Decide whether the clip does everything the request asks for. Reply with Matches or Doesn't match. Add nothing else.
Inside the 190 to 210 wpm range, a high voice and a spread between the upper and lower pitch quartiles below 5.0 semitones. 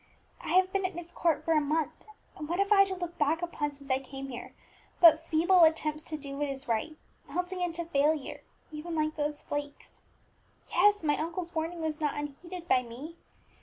Matches